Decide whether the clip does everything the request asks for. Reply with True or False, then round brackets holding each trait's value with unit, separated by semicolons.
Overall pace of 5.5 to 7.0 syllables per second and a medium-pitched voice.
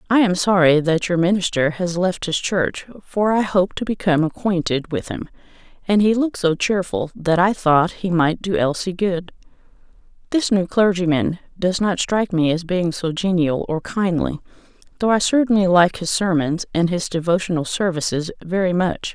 False (5.0 syllables/s; 180 Hz)